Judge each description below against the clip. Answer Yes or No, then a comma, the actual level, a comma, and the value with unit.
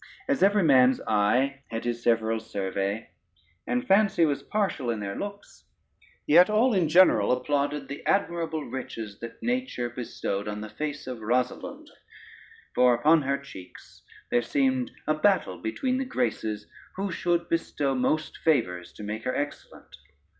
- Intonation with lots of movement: Yes, wide, 7.0 semitones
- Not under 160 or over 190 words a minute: No, average, 150 wpm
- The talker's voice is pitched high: No, low, 135 Hz